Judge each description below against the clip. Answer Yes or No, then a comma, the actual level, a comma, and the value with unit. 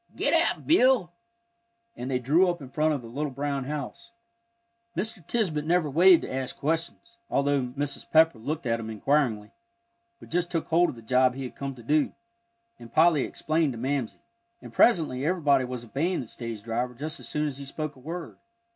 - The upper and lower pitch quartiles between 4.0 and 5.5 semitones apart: Yes, average, 4.3 semitones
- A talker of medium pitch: Yes, medium, 145 Hz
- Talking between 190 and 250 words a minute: Yes, average, 195 wpm